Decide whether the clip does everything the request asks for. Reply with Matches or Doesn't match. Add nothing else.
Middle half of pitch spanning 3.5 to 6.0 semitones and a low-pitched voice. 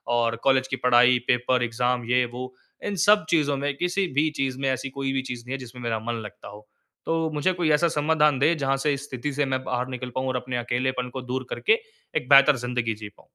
Doesn't match